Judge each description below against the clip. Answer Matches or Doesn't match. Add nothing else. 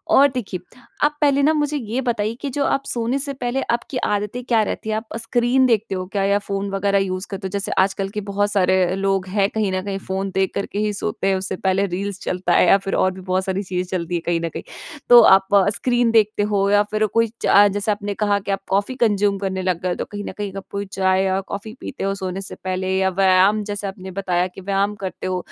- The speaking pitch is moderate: Doesn't match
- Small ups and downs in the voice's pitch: Matches